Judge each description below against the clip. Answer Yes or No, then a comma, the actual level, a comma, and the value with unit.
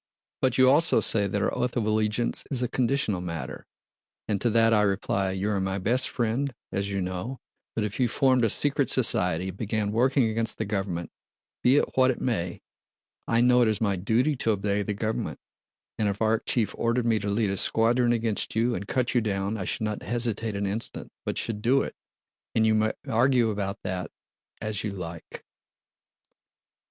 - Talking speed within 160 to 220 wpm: Yes, average, 190 wpm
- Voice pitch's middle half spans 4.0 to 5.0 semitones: No, average, 3.2 semitones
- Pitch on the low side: Yes, low, 110 Hz